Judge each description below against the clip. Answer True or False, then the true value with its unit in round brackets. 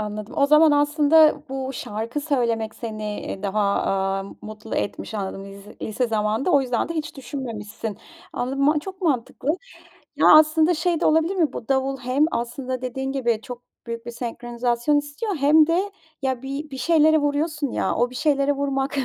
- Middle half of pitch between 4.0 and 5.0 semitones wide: True (4.6 semitones)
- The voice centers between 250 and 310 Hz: True (270 Hz)